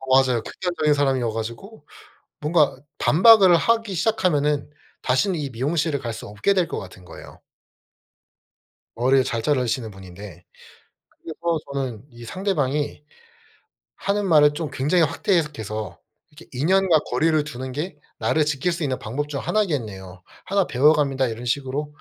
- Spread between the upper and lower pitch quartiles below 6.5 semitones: Yes, average, 5.3 semitones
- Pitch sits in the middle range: Yes, medium, 145 Hz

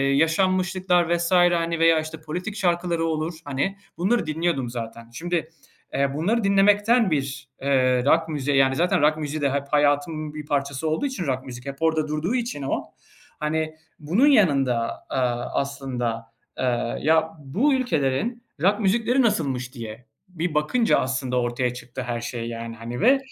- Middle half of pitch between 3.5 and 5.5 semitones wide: Yes, average, 5.0 semitones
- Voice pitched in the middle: Yes, medium, 155 Hz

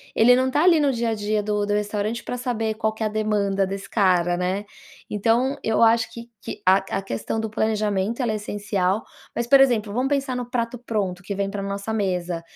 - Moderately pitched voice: No, high, 215 Hz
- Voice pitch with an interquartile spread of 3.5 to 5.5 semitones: No, average, 2.9 semitones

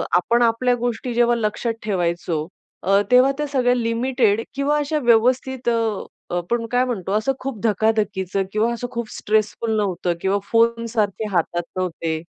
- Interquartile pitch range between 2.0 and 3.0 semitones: No, average, 3.6 semitones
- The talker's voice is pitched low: No, high, 230 Hz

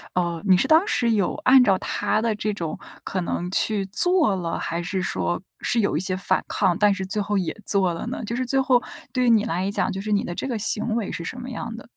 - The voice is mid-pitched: No, high, 205 Hz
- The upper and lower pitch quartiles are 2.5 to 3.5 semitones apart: No, average, 4.3 semitones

